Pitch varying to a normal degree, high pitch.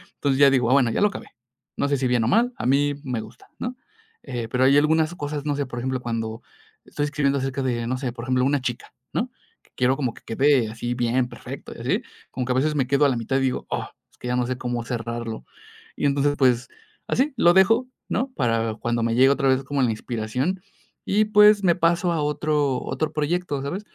No: average, 3.4 semitones; low, 135 Hz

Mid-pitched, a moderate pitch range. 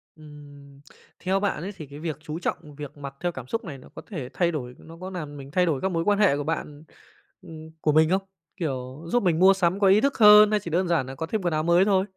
Yes: medium, 165 Hz; average, 4.5 semitones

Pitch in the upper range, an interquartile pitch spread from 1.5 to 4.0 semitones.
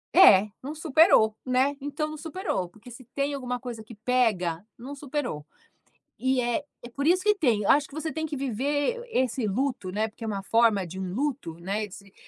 No: very high, 250 Hz; wide, 5.4 semitones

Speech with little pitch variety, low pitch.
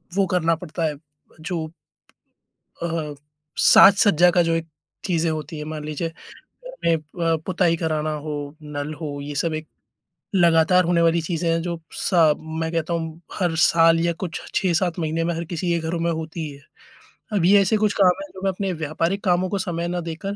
No: narrow, 2.0 semitones; medium, 165 Hz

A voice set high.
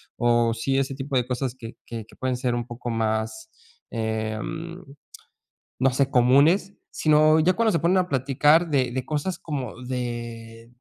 No: low, 130 Hz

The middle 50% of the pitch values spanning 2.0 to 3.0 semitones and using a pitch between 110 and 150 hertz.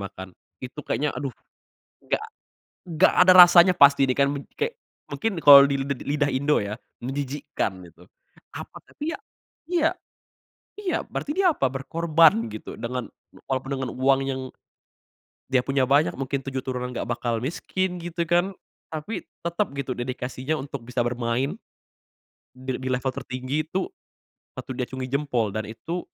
No: average, 4.5 semitones; low, 135 Hz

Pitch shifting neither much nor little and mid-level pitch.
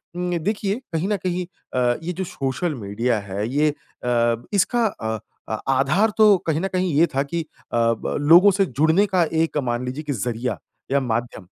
No: wide, 6.8 semitones; medium, 150 Hz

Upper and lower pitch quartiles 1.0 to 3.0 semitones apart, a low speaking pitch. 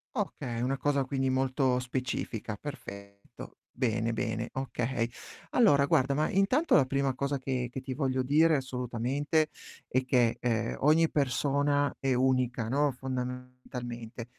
Yes: narrow, 2.4 semitones; low, 130 Hz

